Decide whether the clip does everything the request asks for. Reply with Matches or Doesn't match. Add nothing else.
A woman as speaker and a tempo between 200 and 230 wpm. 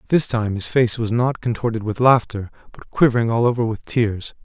Doesn't match